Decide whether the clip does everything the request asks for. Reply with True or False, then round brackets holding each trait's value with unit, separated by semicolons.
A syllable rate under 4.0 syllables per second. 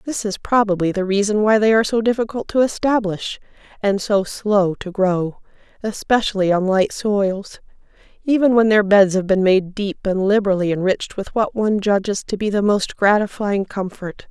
False (5.0 syllables/s)